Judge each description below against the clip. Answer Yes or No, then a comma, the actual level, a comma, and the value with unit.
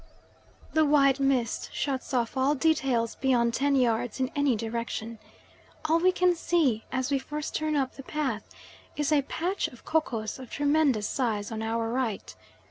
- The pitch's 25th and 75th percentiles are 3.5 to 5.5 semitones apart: Yes, average, 4.2 semitones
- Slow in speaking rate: No, average, 165 wpm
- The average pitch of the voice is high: Yes, very high, 265 Hz